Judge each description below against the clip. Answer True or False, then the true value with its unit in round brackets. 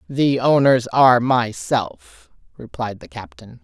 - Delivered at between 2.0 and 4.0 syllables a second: True (3.7 syllables/s)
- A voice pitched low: True (125 Hz)